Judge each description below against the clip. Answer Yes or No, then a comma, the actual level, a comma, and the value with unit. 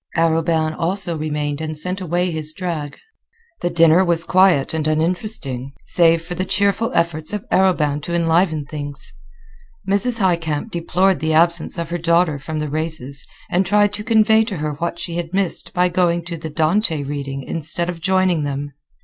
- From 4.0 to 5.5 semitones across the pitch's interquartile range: No, average, 2.8 semitones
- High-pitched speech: No, medium, 170 Hz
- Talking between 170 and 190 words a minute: Yes, average, 175 wpm